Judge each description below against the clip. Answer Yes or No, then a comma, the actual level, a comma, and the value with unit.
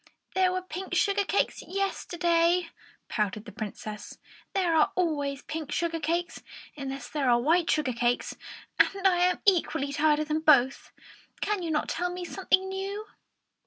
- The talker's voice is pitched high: Yes, very high, 330 Hz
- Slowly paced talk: No, average, 160 wpm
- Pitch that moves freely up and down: No, average, 4.6 semitones